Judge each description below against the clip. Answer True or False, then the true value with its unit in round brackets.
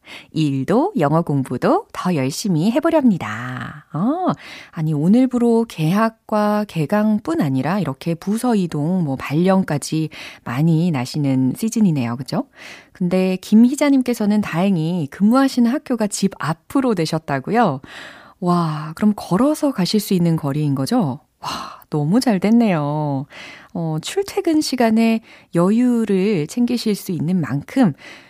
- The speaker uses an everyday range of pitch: False (6.9 semitones)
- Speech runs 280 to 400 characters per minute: False (265 characters per minute)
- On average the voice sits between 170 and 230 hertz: True (190 Hz)